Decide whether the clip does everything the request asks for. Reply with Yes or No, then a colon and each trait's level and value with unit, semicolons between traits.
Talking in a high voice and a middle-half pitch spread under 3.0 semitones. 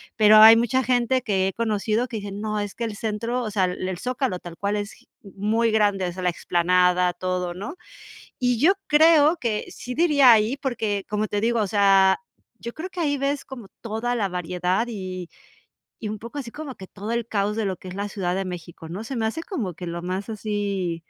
No: high, 210 Hz; average, 4.0 semitones